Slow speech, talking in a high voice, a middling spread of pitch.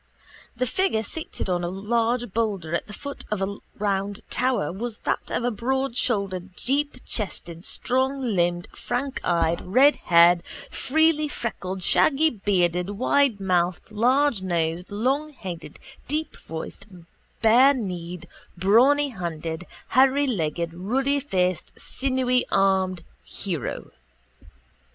No: slow, 85 wpm; high, 210 Hz; wide, 6.5 semitones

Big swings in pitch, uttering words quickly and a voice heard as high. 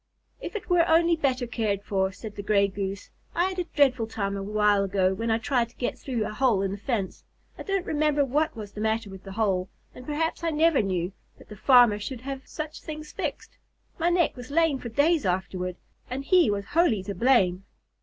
Yes: wide, 7.1 semitones; fast, 220 wpm; high, 230 Hz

